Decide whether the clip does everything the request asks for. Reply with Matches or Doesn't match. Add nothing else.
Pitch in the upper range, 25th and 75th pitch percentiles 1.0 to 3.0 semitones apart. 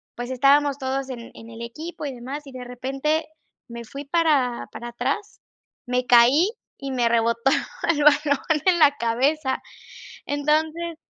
Doesn't match